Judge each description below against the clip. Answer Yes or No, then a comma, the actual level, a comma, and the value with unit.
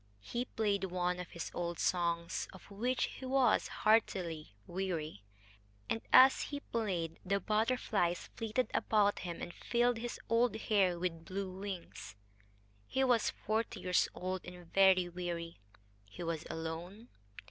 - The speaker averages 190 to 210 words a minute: No, average, 140 wpm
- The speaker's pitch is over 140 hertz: Yes, medium, 185 Hz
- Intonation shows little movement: No, average, 4.4 semitones